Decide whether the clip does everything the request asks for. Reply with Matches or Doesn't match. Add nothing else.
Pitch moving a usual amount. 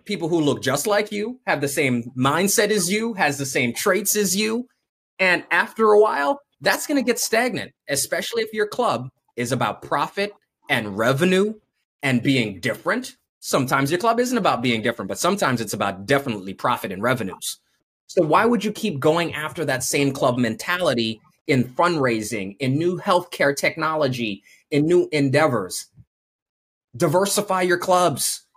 Doesn't match